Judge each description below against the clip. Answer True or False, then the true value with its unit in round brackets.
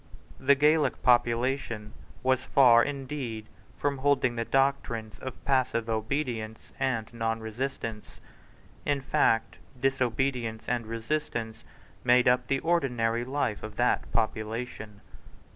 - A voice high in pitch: False (125 Hz)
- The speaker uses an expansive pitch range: False (3.0 semitones)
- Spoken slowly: True (110 wpm)